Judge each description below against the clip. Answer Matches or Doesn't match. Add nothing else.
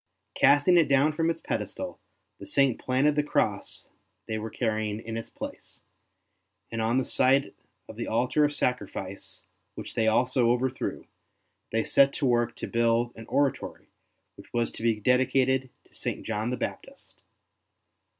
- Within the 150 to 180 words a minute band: Matches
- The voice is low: Matches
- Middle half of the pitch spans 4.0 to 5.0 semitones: Doesn't match